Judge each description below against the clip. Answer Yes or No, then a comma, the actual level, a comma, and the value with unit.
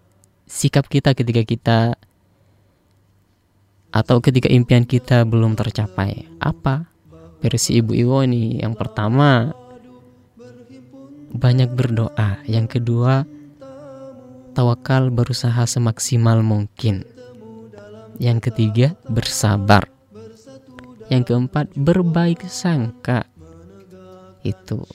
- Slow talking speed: Yes, slow, 80 wpm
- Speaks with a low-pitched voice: Yes, low, 120 Hz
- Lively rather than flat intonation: No, average, 3.3 semitones